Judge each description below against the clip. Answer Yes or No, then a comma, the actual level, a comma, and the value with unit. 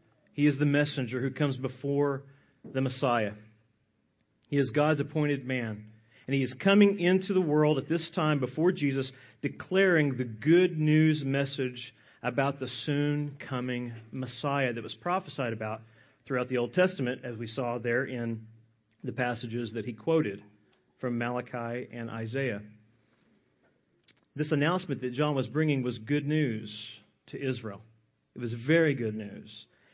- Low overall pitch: Yes, low, 130 Hz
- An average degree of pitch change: Yes, average, 3.9 semitones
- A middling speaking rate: Yes, average, 150 wpm